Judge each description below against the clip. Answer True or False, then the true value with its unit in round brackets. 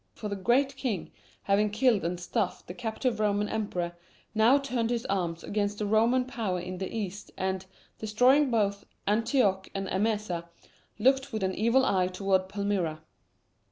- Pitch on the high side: True (210 Hz)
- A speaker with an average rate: True (160 wpm)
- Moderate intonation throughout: True (3.5 semitones)